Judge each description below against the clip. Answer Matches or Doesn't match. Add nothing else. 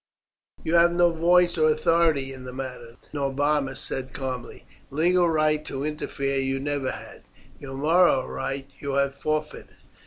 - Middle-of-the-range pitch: Matches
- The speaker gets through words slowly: Doesn't match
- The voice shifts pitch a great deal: Doesn't match